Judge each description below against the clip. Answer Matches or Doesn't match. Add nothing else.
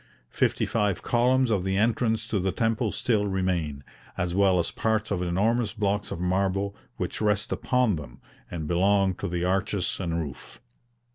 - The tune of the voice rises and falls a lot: Doesn't match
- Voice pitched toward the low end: Matches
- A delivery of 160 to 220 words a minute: Matches